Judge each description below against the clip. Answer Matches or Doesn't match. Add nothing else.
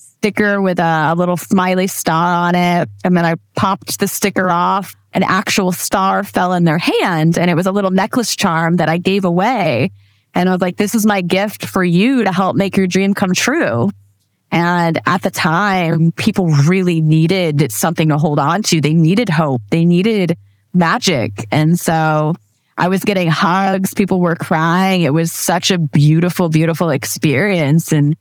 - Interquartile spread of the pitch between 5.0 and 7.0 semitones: Doesn't match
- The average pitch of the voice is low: Doesn't match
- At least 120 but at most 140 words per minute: Doesn't match